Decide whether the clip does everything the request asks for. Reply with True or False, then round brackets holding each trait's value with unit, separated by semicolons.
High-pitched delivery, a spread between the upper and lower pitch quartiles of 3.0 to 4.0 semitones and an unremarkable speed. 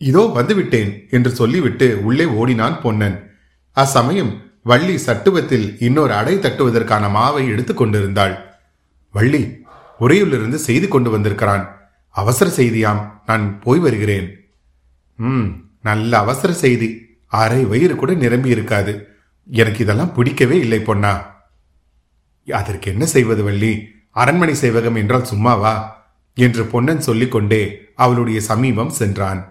False (110 Hz; 3.3 semitones; 110 wpm)